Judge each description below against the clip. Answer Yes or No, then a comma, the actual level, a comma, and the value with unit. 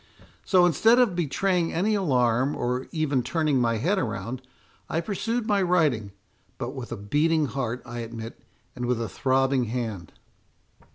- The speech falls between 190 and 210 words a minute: No, average, 155 wpm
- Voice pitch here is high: No, low, 135 Hz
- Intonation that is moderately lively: No, wide, 6.3 semitones